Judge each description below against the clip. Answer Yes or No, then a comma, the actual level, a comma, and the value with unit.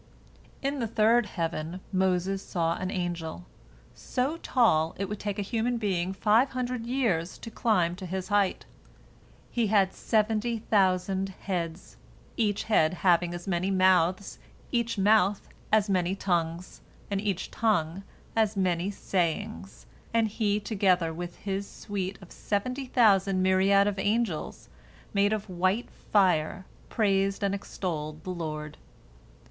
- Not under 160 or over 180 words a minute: No, slow, 135 wpm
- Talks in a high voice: Yes, high, 195 Hz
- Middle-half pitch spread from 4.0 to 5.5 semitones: No, average, 3.2 semitones